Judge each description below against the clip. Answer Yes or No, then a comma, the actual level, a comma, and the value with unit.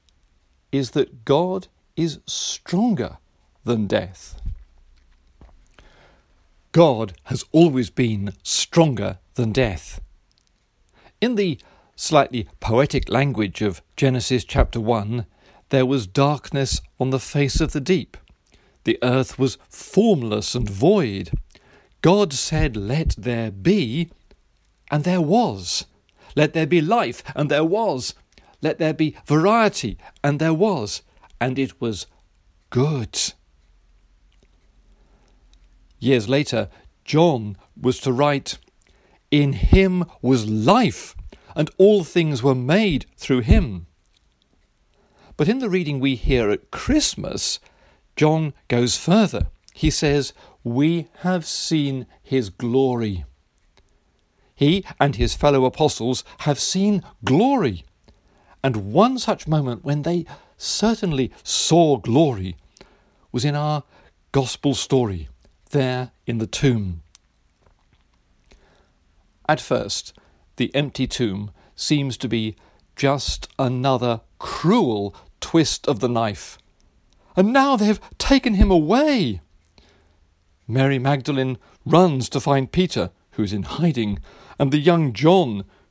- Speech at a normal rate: No, slow, 110 wpm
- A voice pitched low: Yes, low, 130 Hz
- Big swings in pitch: Yes, wide, 7.8 semitones